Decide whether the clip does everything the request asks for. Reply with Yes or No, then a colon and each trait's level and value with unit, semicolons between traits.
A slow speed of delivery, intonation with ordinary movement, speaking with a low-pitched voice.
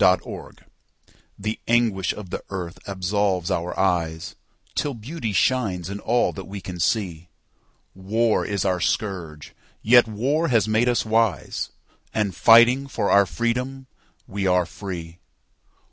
Yes: slow, 125 wpm; average, 4.2 semitones; low, 100 Hz